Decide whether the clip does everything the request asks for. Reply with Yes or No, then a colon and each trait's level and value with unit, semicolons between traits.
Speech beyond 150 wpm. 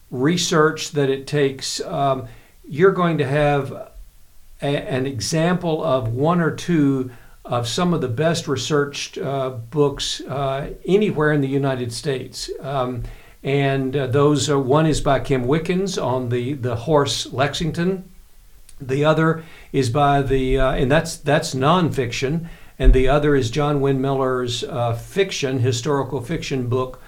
No: average, 145 wpm